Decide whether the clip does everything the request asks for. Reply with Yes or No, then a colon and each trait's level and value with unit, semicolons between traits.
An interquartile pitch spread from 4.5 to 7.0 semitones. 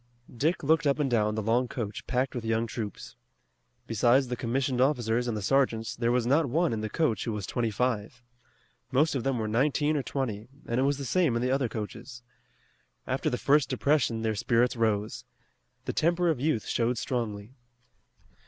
No: average, 3.4 semitones